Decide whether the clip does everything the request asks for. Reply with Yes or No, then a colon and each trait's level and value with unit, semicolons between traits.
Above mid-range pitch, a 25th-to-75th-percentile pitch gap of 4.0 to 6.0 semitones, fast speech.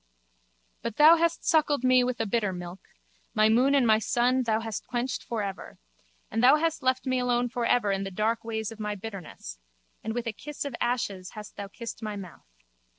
No: high, 230 Hz; average, 3.3 semitones; fast, 210 wpm